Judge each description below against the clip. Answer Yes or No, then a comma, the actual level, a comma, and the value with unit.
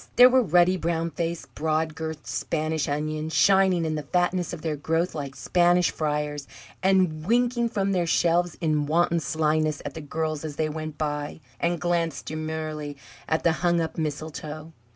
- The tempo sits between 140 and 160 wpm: No, average, 170 wpm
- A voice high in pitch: No, medium, 160 Hz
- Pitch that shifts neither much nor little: No, narrow, 2.1 semitones